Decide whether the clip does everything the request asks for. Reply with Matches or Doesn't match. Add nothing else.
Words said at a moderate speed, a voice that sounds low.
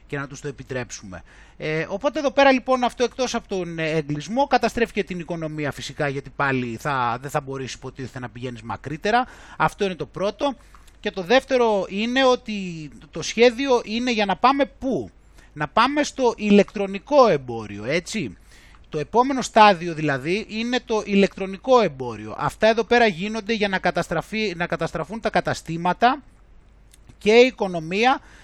Doesn't match